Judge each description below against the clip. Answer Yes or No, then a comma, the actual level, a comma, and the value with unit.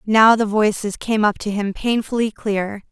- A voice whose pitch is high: Yes, high, 210 Hz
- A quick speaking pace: No, average, 185 wpm